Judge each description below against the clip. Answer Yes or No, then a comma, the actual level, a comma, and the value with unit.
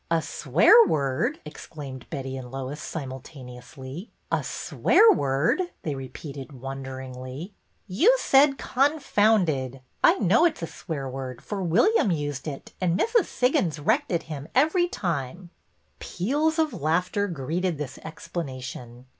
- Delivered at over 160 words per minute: No, average, 140 wpm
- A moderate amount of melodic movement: No, wide, 7.4 semitones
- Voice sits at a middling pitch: Yes, medium, 160 Hz